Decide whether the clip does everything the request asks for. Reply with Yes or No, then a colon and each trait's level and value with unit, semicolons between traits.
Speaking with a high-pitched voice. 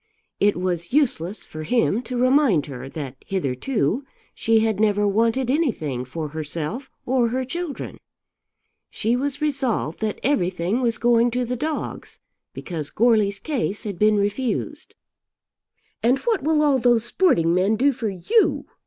Yes: high, 225 Hz